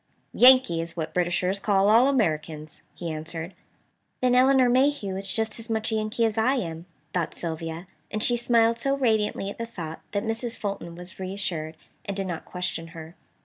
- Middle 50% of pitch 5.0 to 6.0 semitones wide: Yes, wide, 5.5 semitones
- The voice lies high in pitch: Yes, high, 200 Hz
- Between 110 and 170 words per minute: No, average, 185 wpm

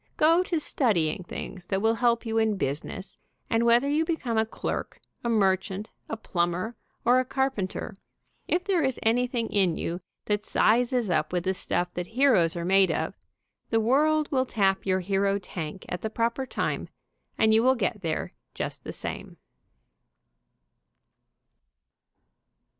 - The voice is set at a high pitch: Yes, high, 220 Hz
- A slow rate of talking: No, average, 155 wpm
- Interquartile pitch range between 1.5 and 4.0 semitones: No, average, 4.8 semitones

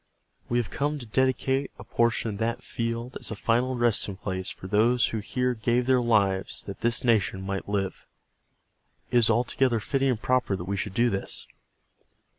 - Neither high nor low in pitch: No, low, 115 Hz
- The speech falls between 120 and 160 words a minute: No, average, 185 wpm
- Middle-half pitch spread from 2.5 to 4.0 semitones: Yes, average, 3.4 semitones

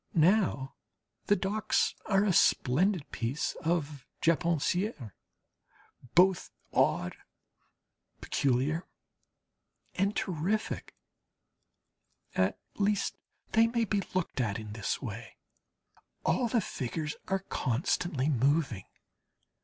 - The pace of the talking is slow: Yes, slow, 90 wpm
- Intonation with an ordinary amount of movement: No, wide, 6.9 semitones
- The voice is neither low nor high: Yes, medium, 165 Hz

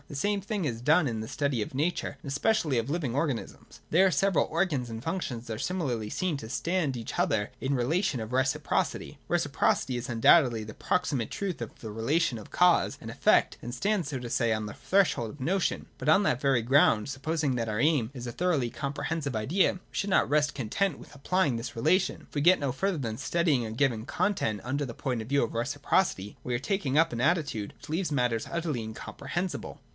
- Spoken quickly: Yes, fast, 220 wpm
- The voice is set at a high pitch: No, medium, 140 Hz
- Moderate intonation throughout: No, wide, 6.3 semitones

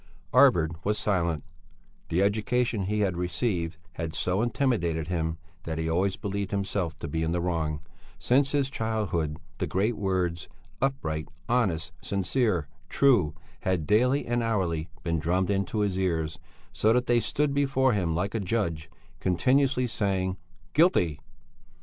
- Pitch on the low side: Yes, very low, 95 Hz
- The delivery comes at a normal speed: Yes, average, 145 wpm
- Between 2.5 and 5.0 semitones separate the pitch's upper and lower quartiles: No, wide, 5.4 semitones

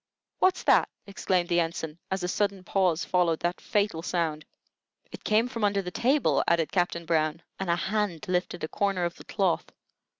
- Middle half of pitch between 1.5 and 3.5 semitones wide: Yes, average, 2.9 semitones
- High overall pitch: No, medium, 180 Hz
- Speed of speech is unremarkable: Yes, average, 180 wpm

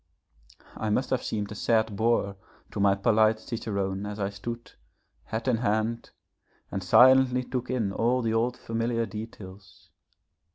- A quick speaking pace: No, average, 150 wpm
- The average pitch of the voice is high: No, low, 110 Hz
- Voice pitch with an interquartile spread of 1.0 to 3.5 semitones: Yes, average, 2.7 semitones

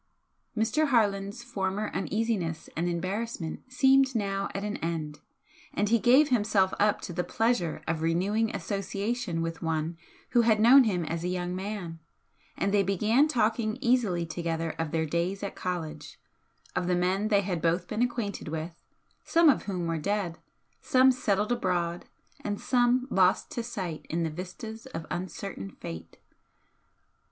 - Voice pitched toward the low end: No, high, 195 Hz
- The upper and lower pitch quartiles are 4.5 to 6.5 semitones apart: Yes, average, 4.8 semitones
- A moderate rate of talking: Yes, average, 155 wpm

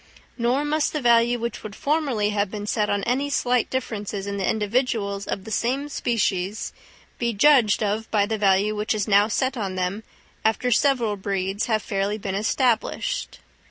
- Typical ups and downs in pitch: Yes, average, 3.5 semitones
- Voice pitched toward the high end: Yes, high, 215 Hz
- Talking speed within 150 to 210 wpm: Yes, average, 175 wpm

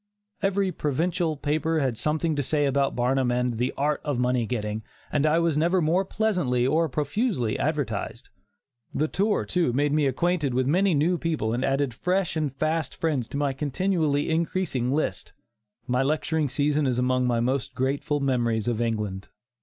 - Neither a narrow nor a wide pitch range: Yes, average, 4.2 semitones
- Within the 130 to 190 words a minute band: Yes, average, 170 wpm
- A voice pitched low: No, medium, 145 Hz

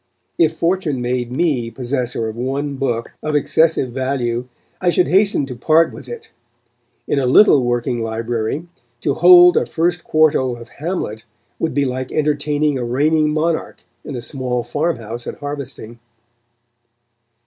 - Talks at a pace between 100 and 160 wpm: Yes, average, 150 wpm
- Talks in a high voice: No, low, 135 Hz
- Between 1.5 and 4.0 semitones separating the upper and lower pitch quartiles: No, average, 4.4 semitones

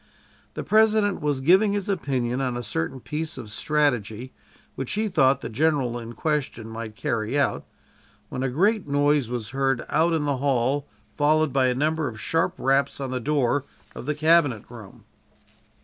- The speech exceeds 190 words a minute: No, average, 175 wpm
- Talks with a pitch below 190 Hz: Yes, medium, 140 Hz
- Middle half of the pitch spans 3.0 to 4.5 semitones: Yes, average, 4.2 semitones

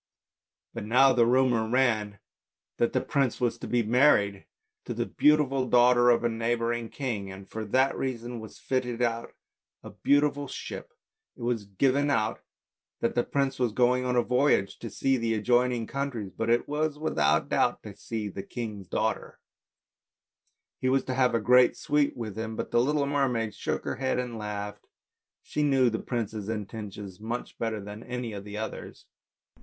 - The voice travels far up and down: No, average, 2.9 semitones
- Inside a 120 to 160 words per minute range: No, average, 175 wpm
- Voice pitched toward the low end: Yes, low, 120 Hz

